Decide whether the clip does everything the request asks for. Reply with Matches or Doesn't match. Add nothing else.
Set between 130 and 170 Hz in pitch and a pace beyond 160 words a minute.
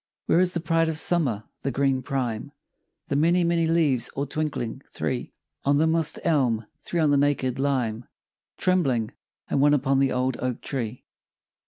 Matches